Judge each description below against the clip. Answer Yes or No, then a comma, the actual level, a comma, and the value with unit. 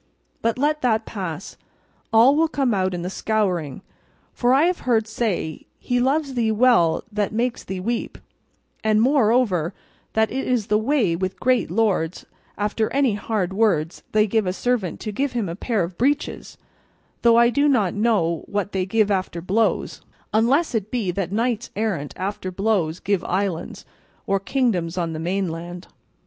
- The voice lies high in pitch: Yes, high, 215 Hz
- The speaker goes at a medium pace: Yes, average, 170 wpm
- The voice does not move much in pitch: No, average, 4.5 semitones